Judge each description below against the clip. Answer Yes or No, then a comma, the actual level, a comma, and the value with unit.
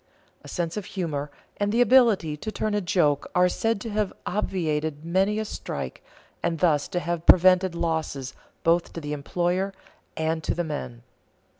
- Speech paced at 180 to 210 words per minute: No, average, 170 wpm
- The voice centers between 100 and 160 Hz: No, medium, 175 Hz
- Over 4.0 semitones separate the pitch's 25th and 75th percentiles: No, average, 3.7 semitones